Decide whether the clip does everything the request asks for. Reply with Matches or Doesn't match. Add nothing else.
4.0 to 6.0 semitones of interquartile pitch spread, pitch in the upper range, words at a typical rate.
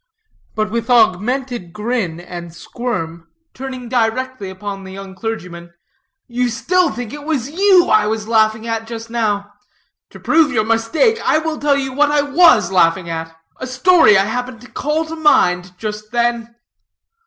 Matches